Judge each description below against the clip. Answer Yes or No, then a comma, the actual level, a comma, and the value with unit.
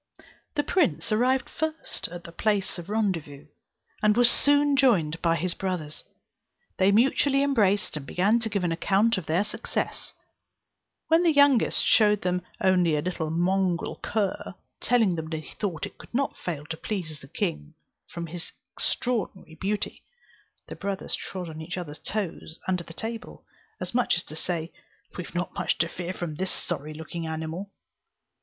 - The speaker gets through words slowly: No, average, 170 wpm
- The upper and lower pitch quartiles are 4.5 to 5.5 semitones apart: Yes, average, 5.0 semitones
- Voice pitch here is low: No, medium, 185 Hz